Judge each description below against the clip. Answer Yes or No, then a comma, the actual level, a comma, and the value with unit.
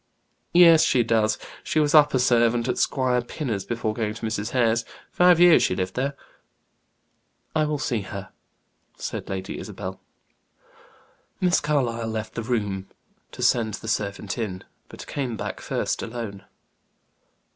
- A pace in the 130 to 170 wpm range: Yes, average, 145 wpm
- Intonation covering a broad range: No, average, 3.9 semitones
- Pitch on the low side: Yes, low, 115 Hz